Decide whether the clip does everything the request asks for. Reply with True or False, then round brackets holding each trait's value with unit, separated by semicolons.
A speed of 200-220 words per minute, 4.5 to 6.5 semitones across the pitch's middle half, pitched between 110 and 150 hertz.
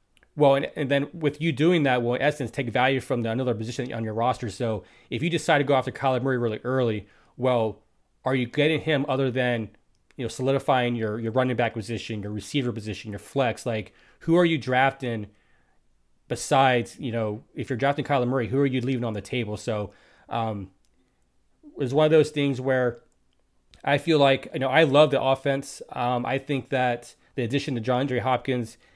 False (205 wpm; 3.2 semitones; 130 Hz)